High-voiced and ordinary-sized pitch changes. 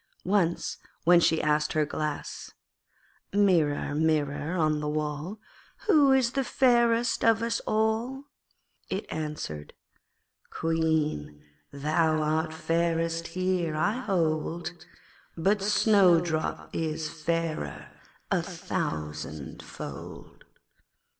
No: medium, 165 Hz; average, 4.5 semitones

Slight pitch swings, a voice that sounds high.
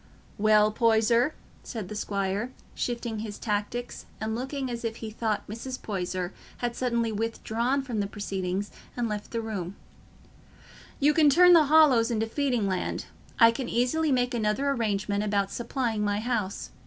No: average, 3.0 semitones; high, 225 Hz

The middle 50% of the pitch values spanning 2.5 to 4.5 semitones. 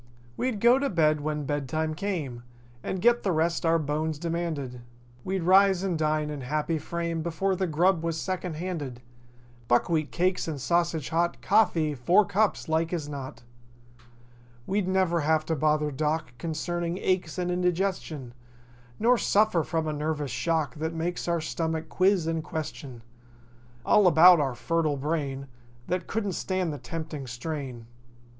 Yes: average, 3.1 semitones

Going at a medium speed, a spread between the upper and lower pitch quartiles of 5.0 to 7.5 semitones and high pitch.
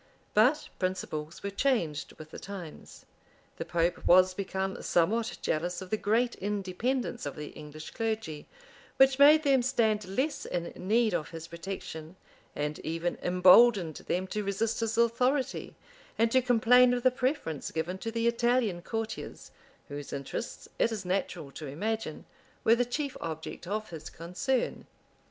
Yes: average, 150 wpm; wide, 5.6 semitones; high, 200 Hz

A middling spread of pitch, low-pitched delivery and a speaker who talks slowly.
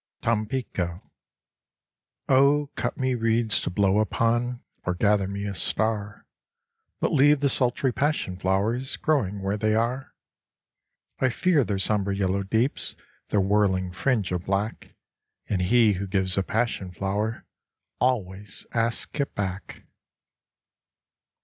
Yes: average, 4.0 semitones; low, 105 Hz; slow, 125 wpm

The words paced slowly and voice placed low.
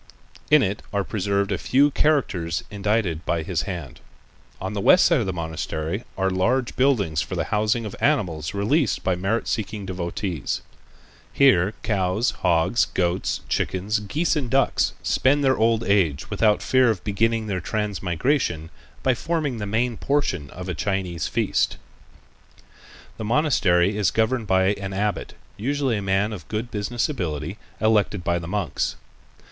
No: average, 155 wpm; low, 100 Hz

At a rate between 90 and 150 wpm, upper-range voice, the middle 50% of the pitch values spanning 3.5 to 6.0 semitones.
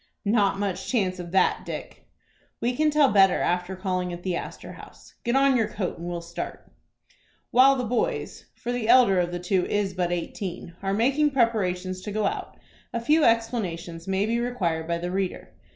No: average, 190 wpm; high, 195 Hz; average, 5.0 semitones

